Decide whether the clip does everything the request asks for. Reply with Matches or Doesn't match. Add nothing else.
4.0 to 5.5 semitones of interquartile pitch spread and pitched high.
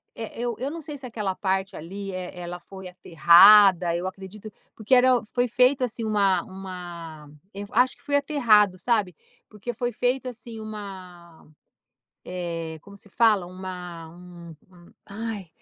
Matches